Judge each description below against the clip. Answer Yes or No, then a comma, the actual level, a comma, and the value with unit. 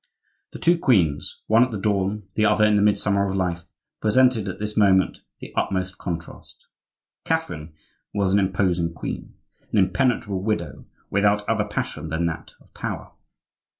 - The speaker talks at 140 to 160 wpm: Yes, average, 150 wpm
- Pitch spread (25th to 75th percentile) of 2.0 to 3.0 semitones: Yes, average, 2.7 semitones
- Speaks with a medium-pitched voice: No, low, 100 Hz